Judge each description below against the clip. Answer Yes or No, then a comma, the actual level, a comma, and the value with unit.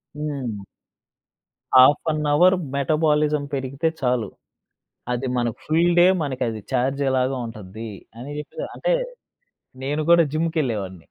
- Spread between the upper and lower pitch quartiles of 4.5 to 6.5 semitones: No, average, 4.1 semitones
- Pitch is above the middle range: No, low, 135 Hz